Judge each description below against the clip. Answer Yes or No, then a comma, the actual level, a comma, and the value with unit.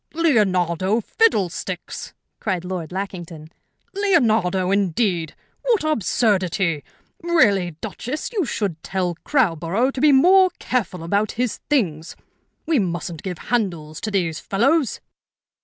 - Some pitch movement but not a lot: No, wide, 6.7 semitones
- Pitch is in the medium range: No, high, 195 Hz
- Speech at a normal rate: No, slow, 110 wpm